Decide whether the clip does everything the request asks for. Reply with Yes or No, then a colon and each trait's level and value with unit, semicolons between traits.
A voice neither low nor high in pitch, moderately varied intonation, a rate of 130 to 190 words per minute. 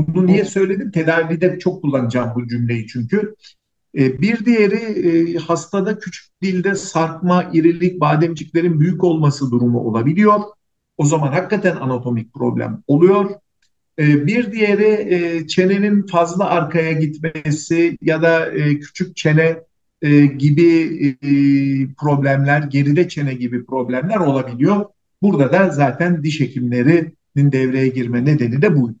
No: medium, 160 Hz; average, 4.5 semitones; average, 110 wpm